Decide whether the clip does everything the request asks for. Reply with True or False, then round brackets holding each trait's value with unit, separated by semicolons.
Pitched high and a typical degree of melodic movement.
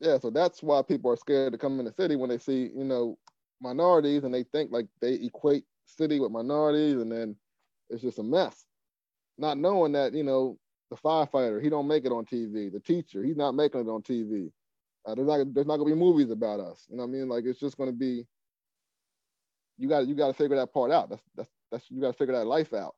False (135 Hz; 3.7 semitones)